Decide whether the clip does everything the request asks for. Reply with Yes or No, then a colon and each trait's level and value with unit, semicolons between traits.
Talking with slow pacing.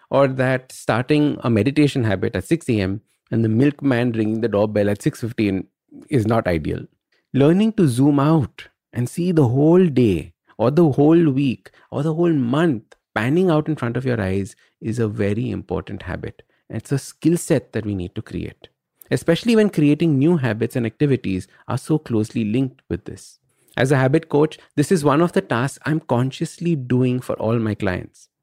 No: average, 185 wpm